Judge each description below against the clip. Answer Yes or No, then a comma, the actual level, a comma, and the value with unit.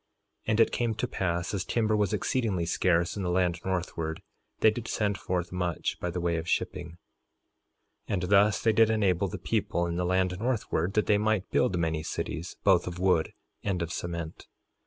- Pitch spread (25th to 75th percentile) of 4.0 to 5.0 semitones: No, average, 3.4 semitones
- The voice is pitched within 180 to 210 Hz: No, very low, 90 Hz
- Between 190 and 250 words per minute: Yes, average, 200 wpm